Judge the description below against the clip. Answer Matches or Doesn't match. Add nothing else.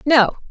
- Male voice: Doesn't match